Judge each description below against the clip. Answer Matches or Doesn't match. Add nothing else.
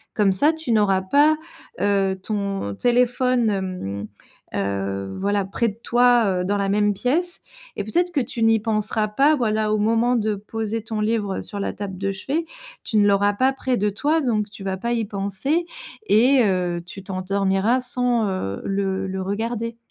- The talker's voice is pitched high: Matches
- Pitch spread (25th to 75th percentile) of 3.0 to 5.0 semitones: Matches